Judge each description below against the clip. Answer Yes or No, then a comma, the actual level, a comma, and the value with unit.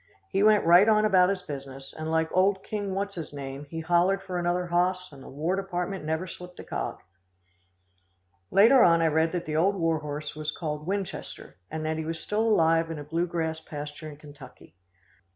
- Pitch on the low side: No, medium, 165 Hz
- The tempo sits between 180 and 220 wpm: Yes, fast, 205 wpm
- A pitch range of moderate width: Yes, average, 3.4 semitones